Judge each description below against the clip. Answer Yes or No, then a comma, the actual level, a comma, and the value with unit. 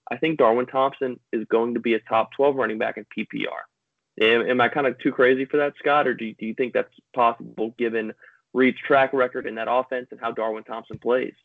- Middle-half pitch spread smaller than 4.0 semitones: Yes, average, 2.8 semitones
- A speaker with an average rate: No, fast, 235 wpm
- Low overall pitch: Yes, low, 120 Hz